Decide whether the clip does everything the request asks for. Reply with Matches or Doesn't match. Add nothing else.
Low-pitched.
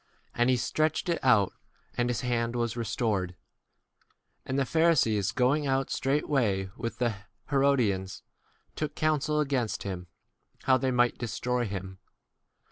Matches